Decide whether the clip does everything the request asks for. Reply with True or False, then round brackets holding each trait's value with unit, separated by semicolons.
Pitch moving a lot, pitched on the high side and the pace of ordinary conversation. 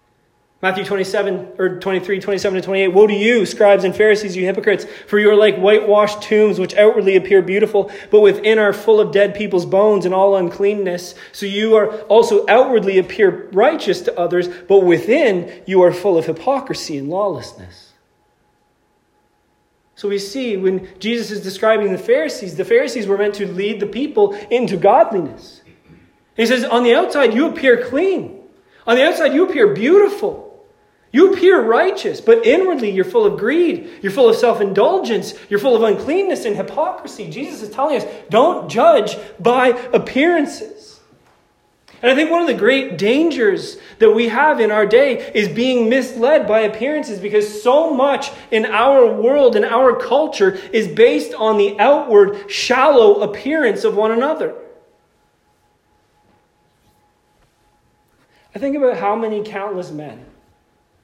True (7.9 semitones; 220 Hz; 155 wpm)